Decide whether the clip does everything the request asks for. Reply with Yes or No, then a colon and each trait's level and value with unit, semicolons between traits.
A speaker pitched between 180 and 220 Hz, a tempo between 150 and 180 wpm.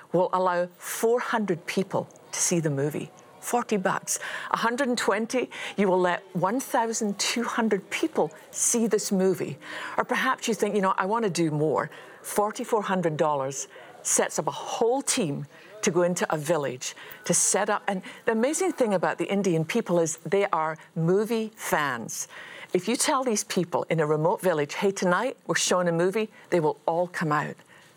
Yes: high, 190 Hz; average, 165 wpm